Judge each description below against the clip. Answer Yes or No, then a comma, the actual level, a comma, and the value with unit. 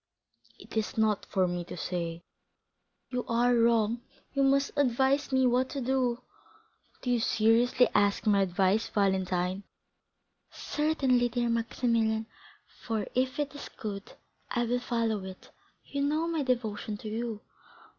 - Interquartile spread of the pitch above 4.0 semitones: No, average, 3.6 semitones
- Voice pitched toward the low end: No, high, 230 Hz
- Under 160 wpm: Yes, average, 140 wpm